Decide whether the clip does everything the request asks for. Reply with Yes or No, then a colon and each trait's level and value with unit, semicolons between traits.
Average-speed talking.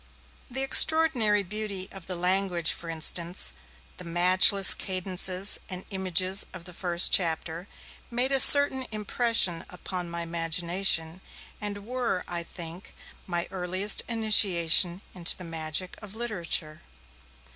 No: slow, 125 wpm